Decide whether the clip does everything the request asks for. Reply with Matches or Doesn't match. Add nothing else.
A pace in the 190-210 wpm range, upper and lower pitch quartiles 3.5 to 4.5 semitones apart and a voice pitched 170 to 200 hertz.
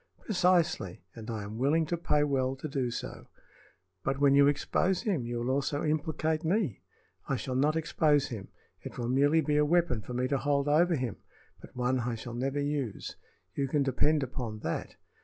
Doesn't match